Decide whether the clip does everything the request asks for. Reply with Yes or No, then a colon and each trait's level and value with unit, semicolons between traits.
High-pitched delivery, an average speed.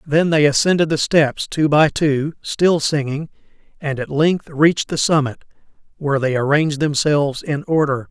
No: medium, 150 Hz; average, 165 wpm